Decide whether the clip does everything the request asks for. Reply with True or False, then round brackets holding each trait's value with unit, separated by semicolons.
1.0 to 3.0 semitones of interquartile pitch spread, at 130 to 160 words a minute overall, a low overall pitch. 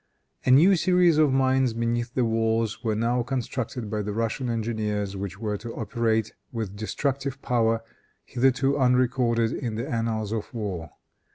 True (2.7 semitones; 155 wpm; 115 Hz)